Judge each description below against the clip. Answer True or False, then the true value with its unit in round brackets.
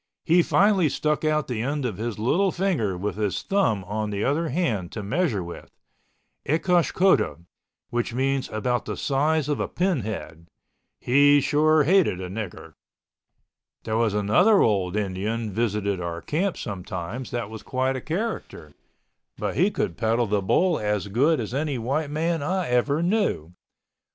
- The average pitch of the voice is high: False (125 Hz)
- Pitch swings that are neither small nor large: False (7.1 semitones)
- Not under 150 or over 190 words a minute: True (160 wpm)